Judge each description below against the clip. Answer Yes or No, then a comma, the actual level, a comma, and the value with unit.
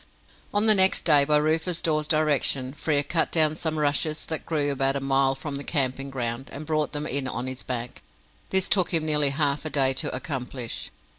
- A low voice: No, medium, 145 Hz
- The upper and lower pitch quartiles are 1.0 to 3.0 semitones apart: Yes, narrow, 2.6 semitones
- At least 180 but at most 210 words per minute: Yes, fast, 205 wpm